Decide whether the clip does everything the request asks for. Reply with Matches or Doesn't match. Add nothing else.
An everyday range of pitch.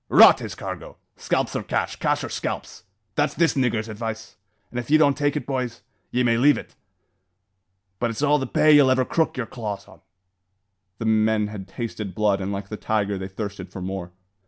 Matches